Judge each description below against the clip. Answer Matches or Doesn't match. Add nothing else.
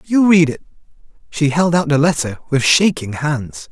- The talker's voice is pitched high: Doesn't match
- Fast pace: Doesn't match